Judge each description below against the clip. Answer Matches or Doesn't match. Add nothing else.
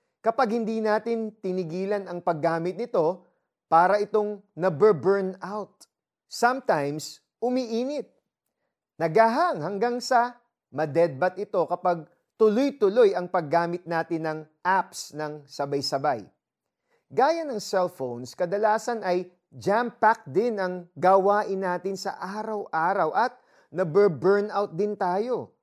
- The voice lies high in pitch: Matches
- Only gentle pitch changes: Doesn't match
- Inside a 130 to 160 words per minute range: Doesn't match